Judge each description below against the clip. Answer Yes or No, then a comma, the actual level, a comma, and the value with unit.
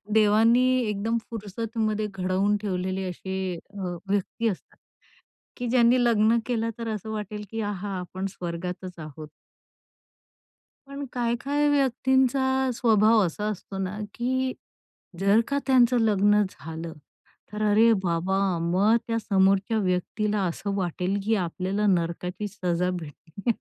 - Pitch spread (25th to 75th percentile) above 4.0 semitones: No, average, 3.6 semitones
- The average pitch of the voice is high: Yes, high, 210 Hz